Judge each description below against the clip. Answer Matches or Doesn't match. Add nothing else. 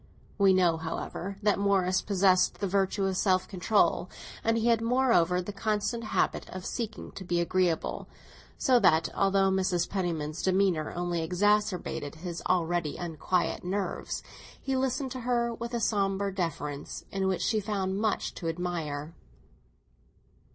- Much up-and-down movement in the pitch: Doesn't match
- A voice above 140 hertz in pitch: Matches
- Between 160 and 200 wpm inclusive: Doesn't match